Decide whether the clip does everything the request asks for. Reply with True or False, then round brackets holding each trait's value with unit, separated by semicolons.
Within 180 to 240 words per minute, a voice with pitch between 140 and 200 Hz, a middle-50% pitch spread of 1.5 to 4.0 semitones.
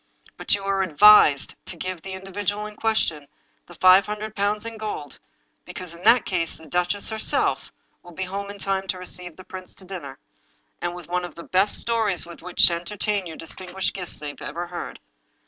True (200 wpm; 185 Hz; 2.7 semitones)